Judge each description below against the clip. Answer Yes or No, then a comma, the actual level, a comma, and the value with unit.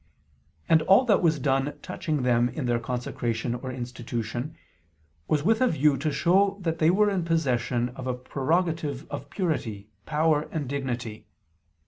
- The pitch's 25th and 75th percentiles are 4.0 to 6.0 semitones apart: Yes, average, 4.9 semitones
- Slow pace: No, average, 155 wpm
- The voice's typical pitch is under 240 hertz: Yes, medium, 140 Hz